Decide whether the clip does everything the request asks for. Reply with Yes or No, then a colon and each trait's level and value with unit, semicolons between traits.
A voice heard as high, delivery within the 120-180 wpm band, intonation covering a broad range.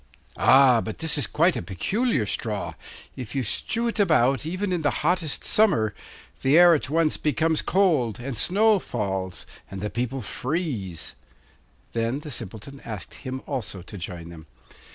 No: low, 135 Hz; average, 160 wpm; wide, 7.5 semitones